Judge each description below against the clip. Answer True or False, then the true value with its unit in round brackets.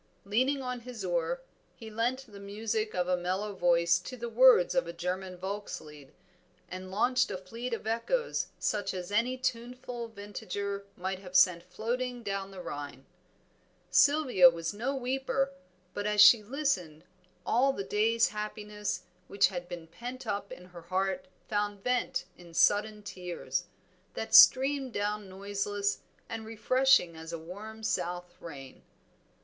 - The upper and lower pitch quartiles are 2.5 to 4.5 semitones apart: False (5.0 semitones)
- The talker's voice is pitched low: False (205 Hz)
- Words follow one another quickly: False (150 wpm)